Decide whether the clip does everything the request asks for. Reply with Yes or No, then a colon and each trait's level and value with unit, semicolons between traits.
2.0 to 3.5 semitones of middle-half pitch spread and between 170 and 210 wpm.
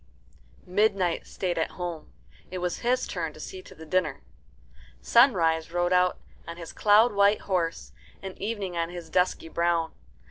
No: average, 2.8 semitones; average, 155 wpm